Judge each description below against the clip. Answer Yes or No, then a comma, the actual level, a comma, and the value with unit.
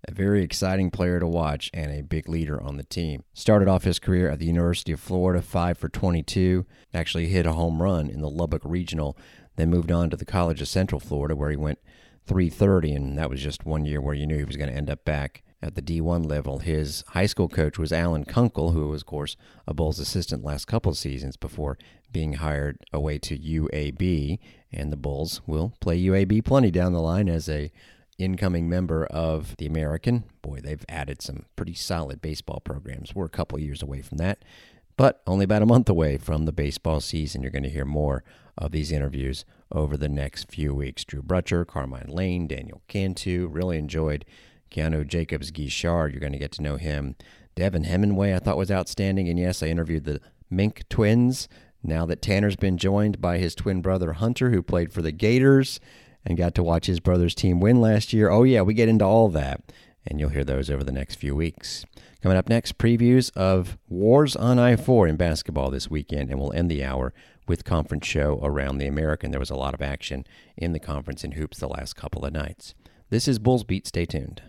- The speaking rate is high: Yes, fast, 210 wpm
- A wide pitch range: No, average, 4.1 semitones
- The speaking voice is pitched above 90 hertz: No, very low, 85 Hz